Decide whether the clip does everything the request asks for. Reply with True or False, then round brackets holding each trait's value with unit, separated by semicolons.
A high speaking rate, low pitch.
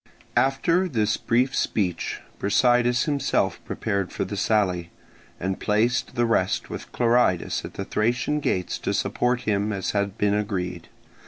False (145 wpm; 110 Hz)